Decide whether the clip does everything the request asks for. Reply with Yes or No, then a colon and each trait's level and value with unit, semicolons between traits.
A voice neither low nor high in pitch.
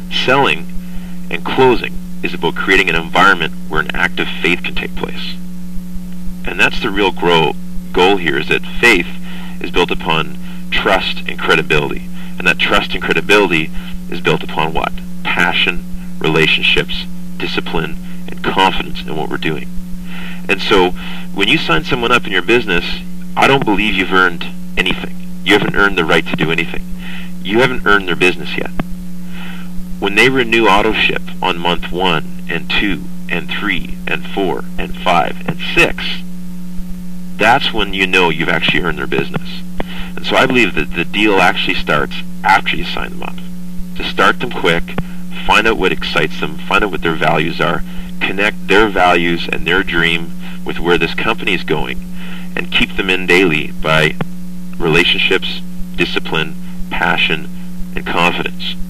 Yes: medium, 180 Hz